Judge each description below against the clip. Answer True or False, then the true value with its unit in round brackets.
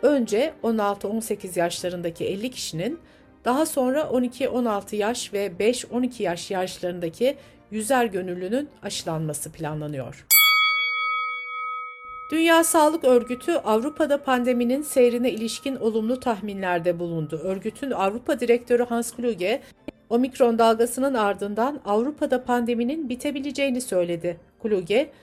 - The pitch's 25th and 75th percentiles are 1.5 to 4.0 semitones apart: False (5.4 semitones)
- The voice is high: True (240 Hz)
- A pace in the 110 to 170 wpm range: False (95 wpm)